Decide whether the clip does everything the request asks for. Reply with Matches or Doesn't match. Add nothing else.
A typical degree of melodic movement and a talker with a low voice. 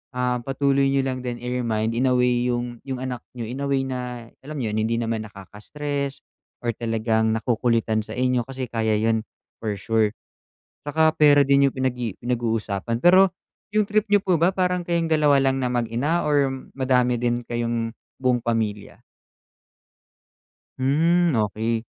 Matches